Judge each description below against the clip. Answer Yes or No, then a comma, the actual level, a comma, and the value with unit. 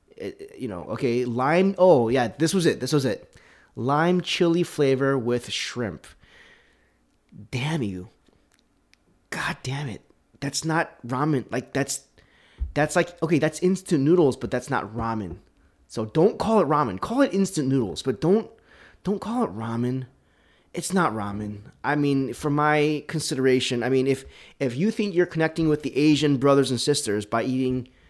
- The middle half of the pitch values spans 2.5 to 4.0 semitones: No, average, 4.9 semitones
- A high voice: No, medium, 140 Hz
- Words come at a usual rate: Yes, average, 160 wpm